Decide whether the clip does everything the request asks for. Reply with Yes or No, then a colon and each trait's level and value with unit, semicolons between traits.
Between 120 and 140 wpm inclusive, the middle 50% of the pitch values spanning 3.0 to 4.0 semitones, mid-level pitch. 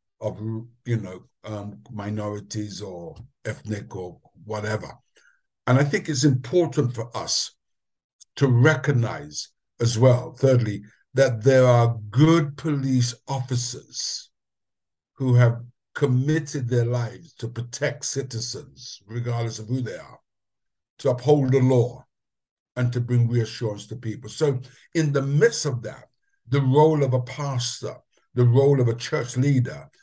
No: slow, 135 wpm; average, 3.4 semitones; low, 125 Hz